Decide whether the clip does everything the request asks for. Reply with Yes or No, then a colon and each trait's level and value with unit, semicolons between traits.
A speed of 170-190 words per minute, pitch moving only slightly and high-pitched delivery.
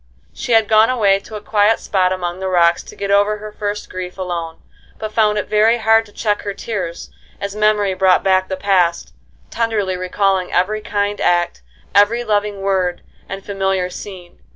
Yes: average, 180 wpm; narrow, 2.3 semitones; high, 200 Hz